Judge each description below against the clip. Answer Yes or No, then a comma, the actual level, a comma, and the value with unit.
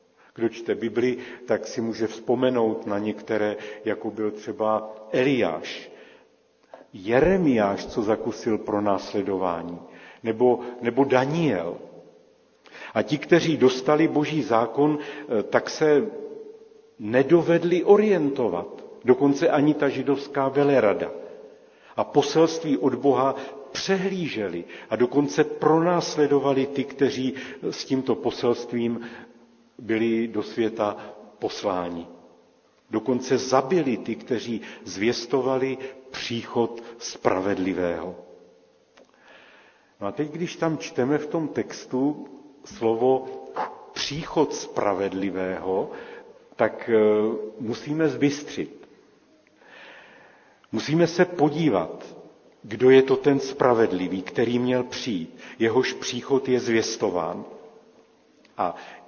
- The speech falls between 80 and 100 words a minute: Yes, slow, 90 wpm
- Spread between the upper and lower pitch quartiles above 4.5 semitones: Yes, average, 5.1 semitones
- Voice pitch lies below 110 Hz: No, low, 130 Hz